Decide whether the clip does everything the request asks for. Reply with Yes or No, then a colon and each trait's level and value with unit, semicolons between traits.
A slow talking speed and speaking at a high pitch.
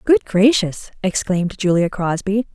Yes: slow, 120 wpm; high, 195 Hz